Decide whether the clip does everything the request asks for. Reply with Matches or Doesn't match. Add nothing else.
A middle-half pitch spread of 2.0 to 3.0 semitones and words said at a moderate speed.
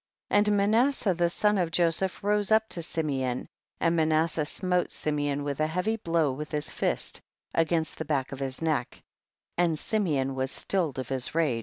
Doesn't match